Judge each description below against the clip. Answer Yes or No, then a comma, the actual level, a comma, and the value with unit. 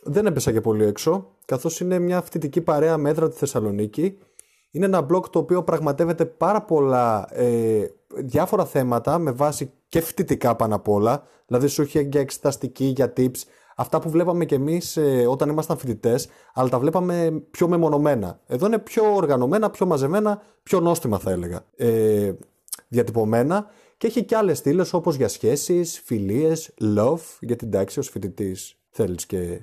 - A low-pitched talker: No, medium, 150 Hz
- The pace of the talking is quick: Yes, fast, 175 wpm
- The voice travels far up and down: Yes, wide, 6.7 semitones